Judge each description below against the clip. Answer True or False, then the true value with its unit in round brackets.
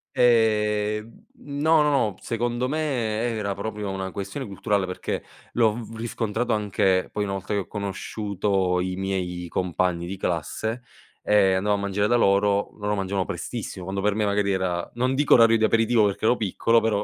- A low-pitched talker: True (105 Hz)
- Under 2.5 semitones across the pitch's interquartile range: False (2.9 semitones)